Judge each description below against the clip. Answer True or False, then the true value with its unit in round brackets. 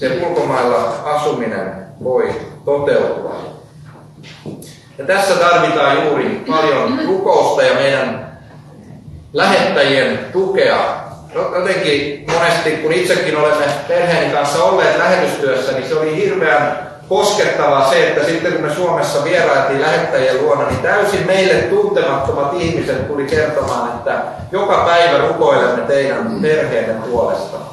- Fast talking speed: False (115 wpm)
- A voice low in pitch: False (175 Hz)